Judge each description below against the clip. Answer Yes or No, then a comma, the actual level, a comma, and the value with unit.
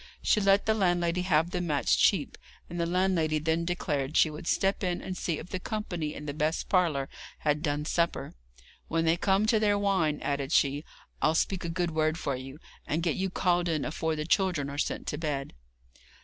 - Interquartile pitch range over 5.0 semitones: No, average, 3.2 semitones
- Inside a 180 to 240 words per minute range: Yes, fast, 205 wpm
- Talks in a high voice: No, medium, 165 Hz